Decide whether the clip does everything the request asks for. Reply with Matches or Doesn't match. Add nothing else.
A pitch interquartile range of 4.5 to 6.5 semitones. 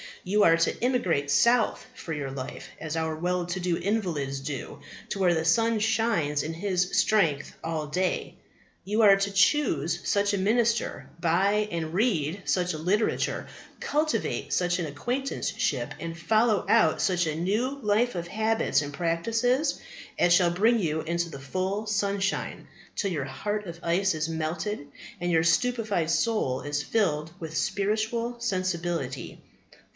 Matches